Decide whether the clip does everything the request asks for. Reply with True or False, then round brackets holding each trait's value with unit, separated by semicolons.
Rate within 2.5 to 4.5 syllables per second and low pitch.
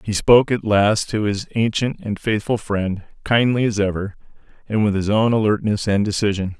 False (5.1 syllables/s; 105 Hz)